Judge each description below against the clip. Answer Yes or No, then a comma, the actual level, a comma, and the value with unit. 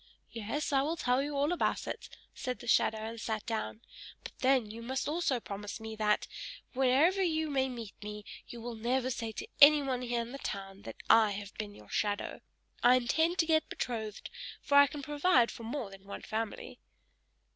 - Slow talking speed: No, average, 195 wpm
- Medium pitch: No, high, 245 Hz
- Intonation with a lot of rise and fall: No, average, 4.5 semitones